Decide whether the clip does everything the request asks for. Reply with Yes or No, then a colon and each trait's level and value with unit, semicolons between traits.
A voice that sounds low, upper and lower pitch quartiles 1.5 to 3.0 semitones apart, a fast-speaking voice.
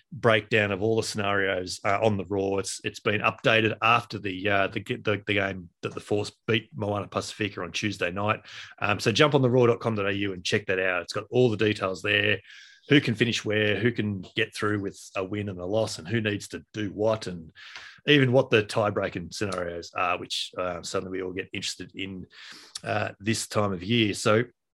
Yes: low, 105 Hz; narrow, 2.4 semitones; fast, 210 wpm